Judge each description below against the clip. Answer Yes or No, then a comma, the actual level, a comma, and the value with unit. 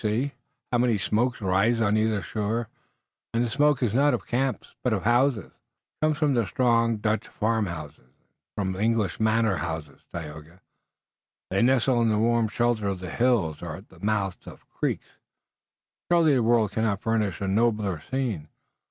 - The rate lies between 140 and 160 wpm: No, average, 170 wpm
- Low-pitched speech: Yes, low, 110 Hz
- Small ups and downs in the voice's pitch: No, average, 3.5 semitones